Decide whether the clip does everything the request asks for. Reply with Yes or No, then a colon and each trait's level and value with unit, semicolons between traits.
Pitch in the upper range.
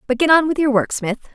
Yes: very high, 265 Hz